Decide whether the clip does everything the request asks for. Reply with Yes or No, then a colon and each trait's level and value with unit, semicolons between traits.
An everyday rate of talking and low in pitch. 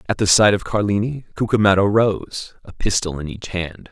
Yes: average, 185 wpm; low, 100 Hz